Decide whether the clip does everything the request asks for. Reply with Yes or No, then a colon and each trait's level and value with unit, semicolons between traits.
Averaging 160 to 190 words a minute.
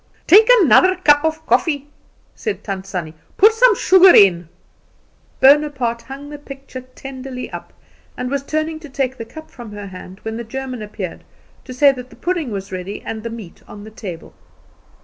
Yes: average, 180 wpm